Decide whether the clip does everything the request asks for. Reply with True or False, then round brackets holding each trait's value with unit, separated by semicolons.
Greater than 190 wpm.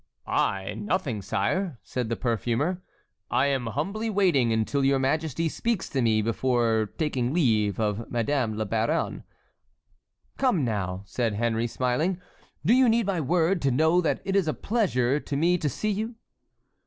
False (160 wpm)